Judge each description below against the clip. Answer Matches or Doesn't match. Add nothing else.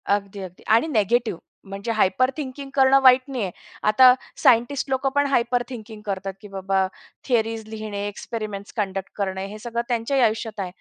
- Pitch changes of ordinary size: Matches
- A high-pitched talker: Matches